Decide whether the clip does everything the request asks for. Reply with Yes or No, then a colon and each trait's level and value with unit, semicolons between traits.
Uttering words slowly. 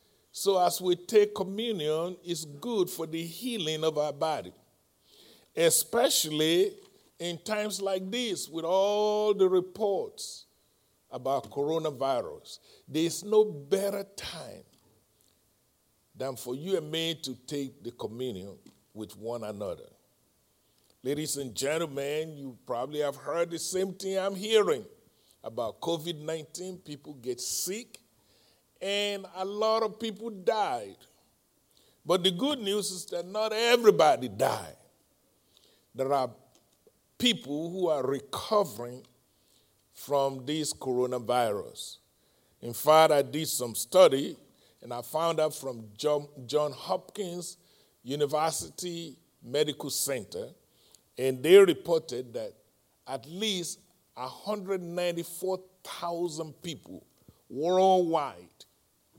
Yes: slow, 105 wpm